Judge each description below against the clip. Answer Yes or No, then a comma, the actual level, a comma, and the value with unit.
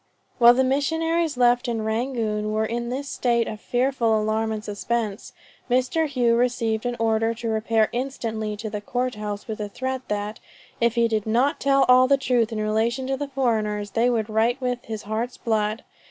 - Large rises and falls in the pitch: No, narrow, 2.6 semitones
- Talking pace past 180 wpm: Yes, average, 190 wpm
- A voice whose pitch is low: No, high, 235 Hz